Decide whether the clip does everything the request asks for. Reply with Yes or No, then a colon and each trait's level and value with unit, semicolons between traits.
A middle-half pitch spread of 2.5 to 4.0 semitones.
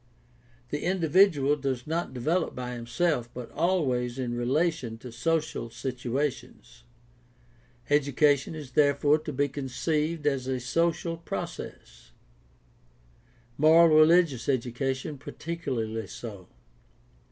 No: average, 4.4 semitones